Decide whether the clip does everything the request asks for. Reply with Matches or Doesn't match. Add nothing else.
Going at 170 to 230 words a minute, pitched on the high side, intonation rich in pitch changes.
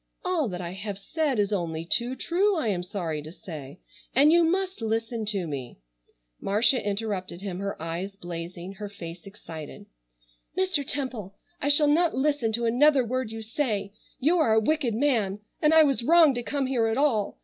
Matches